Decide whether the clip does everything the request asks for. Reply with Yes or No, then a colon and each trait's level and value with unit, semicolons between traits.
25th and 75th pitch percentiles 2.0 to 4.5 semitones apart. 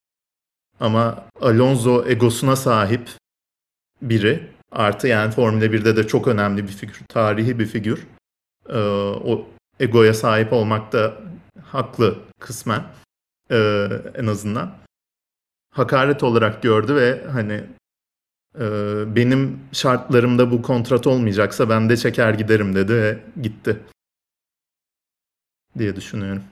Yes: average, 2.9 semitones